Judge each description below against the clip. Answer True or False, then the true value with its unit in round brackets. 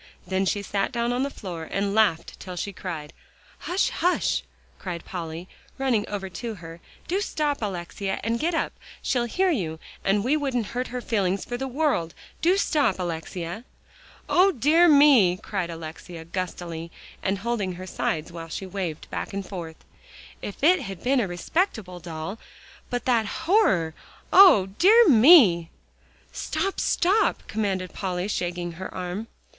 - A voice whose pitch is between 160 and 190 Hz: False (200 Hz)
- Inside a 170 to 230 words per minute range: False (155 wpm)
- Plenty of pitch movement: True (6.7 semitones)